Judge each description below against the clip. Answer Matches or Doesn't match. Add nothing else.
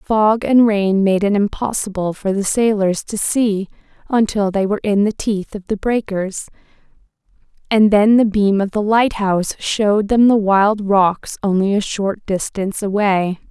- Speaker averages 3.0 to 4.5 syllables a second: Matches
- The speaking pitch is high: Matches